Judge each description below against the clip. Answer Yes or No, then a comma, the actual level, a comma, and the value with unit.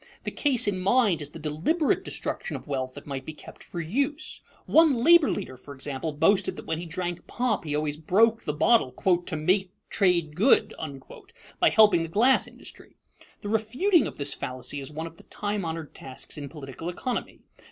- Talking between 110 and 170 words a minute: No, average, 190 wpm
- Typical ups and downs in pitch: No, wide, 6.7 semitones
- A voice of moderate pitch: Yes, medium, 175 Hz